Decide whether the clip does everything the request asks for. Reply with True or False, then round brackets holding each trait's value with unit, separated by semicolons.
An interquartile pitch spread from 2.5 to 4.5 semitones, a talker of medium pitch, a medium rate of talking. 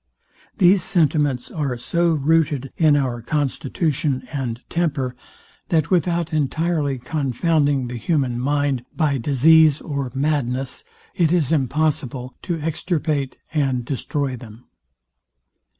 False (3.5 semitones; 145 Hz; 110 wpm)